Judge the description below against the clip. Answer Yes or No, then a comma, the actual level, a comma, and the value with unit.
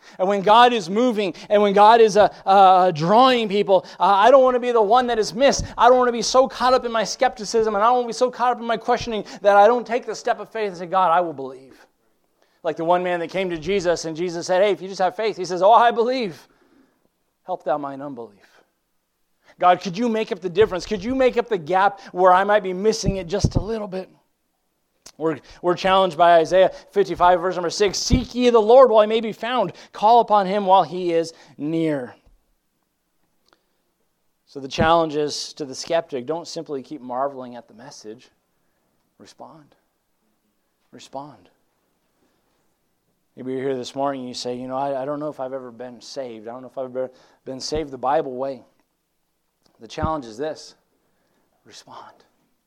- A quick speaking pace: Yes, fast, 210 wpm